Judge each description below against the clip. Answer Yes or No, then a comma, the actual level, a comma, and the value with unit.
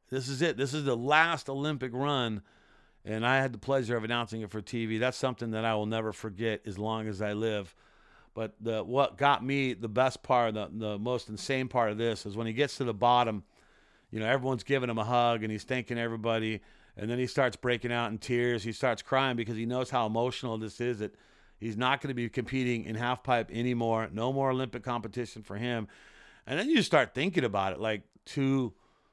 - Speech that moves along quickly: Yes, fast, 220 wpm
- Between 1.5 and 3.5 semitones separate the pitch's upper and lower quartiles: Yes, average, 2.7 semitones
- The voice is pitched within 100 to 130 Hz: Yes, low, 120 Hz